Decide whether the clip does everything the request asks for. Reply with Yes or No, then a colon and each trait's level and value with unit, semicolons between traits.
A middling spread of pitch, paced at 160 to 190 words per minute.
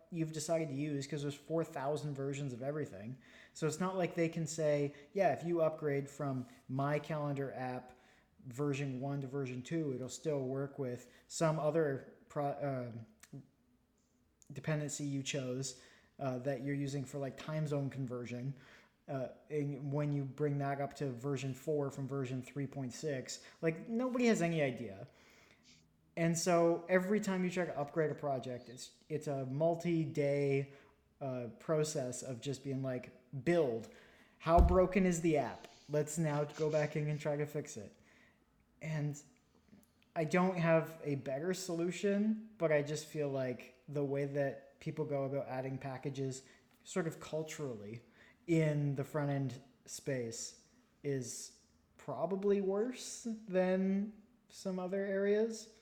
No: average, 3.5 semitones; average, 150 wpm